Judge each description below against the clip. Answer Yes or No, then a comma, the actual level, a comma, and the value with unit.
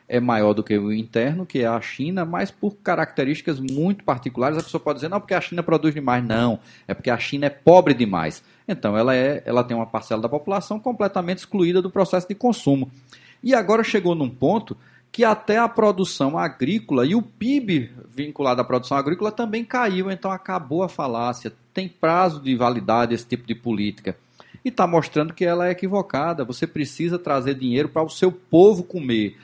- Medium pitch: Yes, medium, 155 Hz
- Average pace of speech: No, fast, 190 wpm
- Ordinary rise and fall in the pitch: No, wide, 7.1 semitones